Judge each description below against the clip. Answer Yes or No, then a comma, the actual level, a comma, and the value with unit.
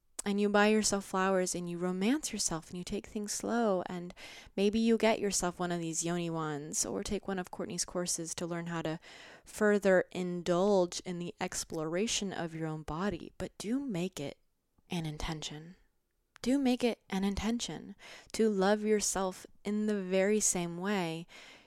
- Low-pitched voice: No, high, 190 Hz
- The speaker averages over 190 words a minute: No, average, 170 wpm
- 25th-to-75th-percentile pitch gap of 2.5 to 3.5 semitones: Yes, average, 3.2 semitones